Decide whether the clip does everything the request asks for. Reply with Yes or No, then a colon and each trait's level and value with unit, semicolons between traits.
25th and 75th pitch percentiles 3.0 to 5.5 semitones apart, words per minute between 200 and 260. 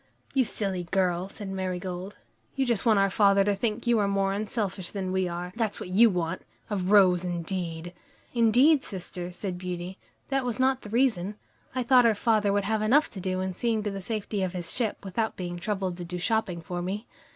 Yes: average, 3.4 semitones; fast, 205 wpm